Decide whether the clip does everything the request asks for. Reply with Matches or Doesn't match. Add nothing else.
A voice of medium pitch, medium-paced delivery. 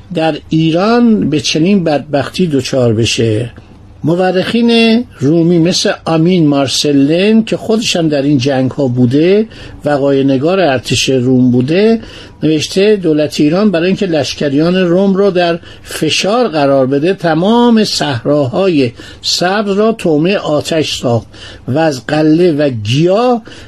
Matches